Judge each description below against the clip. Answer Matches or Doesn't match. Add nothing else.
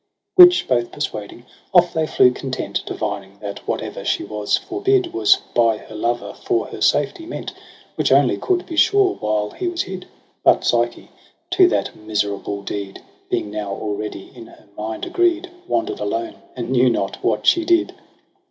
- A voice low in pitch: Matches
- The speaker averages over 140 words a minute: Matches